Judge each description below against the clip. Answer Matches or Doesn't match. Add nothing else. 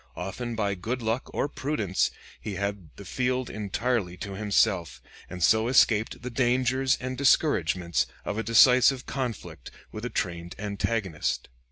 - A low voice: Matches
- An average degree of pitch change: Matches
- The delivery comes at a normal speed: Matches